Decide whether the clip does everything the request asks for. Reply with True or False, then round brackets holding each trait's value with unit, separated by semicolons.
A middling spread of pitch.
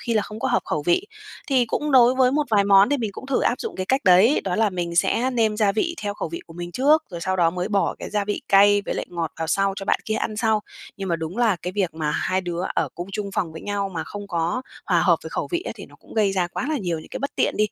True (4.4 semitones)